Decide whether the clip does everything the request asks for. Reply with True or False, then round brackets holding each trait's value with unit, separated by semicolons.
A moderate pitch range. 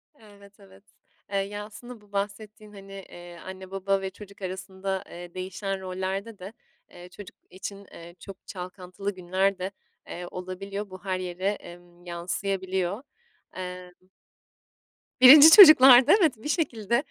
False (2.0 semitones)